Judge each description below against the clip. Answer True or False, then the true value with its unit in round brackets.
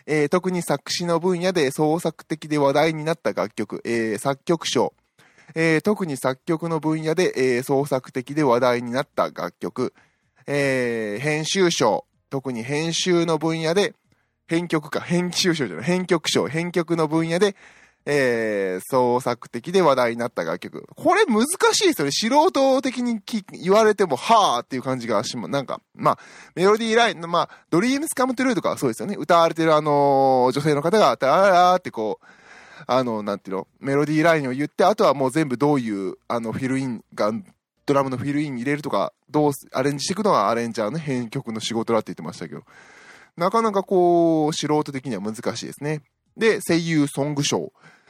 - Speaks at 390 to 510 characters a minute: False (360 characters per minute)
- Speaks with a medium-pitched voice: True (150 Hz)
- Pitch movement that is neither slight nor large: True (5.0 semitones)